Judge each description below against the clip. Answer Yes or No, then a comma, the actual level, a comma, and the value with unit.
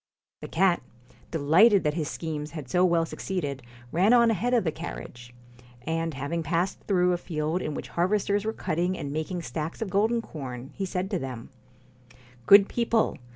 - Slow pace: No, average, 180 wpm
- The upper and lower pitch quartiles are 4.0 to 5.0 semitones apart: Yes, average, 4.4 semitones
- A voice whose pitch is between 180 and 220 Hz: No, medium, 170 Hz